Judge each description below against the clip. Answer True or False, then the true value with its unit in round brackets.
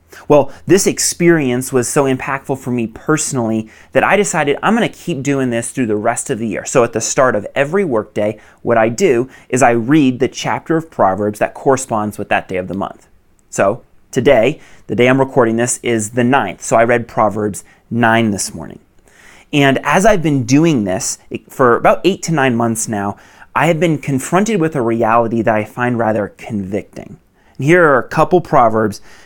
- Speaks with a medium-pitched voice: False (125 Hz)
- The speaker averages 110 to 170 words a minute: False (200 wpm)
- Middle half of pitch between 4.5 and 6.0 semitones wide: True (5.1 semitones)